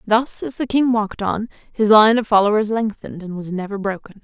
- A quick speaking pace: Yes, fast, 210 wpm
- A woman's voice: Yes, female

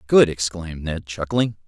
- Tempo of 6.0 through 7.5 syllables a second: No, 4.9 syllables/s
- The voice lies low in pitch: Yes, very low, 95 Hz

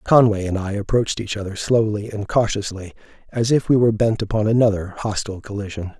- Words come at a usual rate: Yes, average, 180 wpm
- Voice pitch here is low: Yes, low, 105 Hz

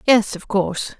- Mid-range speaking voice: No, high, 205 Hz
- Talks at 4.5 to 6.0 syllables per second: Yes, 4.8 syllables/s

